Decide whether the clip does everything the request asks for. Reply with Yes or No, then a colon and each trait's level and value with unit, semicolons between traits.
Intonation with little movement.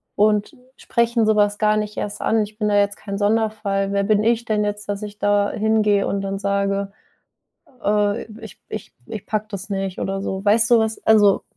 Yes: narrow, 1.4 semitones